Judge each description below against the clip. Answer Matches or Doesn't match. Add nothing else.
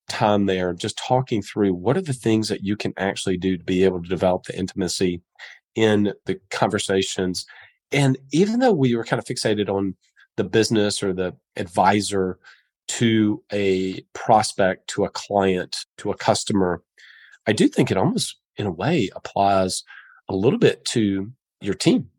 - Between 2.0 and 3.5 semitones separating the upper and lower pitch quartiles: Matches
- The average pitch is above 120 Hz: Doesn't match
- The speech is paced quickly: Doesn't match